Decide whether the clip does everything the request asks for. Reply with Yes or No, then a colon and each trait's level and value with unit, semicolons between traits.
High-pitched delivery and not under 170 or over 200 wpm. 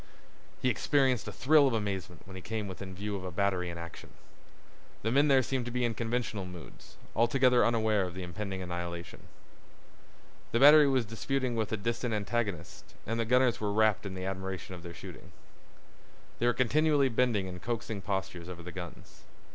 No: low, 105 Hz; average, 180 wpm